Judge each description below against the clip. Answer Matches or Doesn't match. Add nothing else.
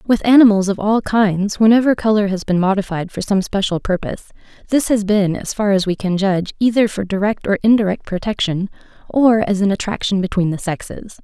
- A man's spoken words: Doesn't match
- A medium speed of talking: Matches